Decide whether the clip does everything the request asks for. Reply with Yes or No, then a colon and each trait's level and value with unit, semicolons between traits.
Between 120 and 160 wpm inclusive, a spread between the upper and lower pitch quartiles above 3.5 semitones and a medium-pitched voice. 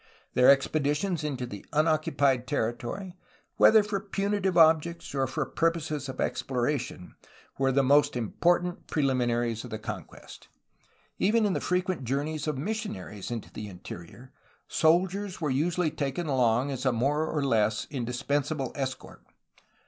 Yes: average, 140 wpm; average, 5.0 semitones; medium, 145 Hz